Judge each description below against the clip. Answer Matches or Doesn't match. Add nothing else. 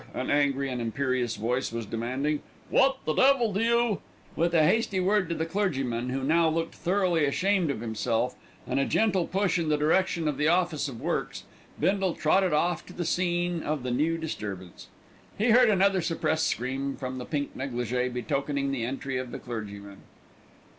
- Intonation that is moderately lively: Doesn't match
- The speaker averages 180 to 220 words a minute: Matches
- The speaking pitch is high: Doesn't match